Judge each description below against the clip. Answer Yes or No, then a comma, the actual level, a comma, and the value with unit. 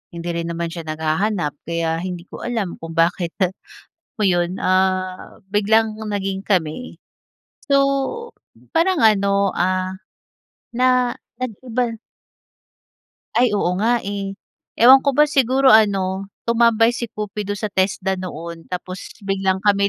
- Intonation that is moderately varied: Yes, average, 4.2 semitones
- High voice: Yes, high, 200 Hz